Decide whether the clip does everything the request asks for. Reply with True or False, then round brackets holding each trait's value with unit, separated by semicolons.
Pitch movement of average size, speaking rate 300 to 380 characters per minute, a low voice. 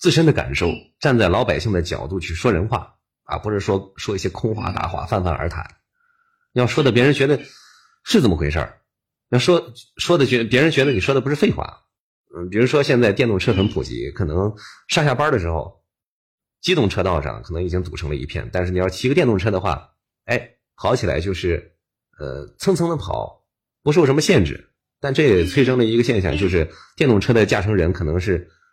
False (6.8 semitones; 305 characters per minute; 105 Hz)